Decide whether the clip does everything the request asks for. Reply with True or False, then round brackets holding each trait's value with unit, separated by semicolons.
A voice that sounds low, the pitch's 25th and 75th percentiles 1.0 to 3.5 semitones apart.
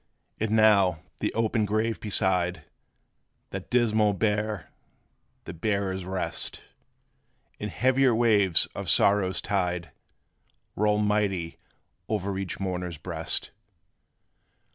True (100 Hz; 2.9 semitones)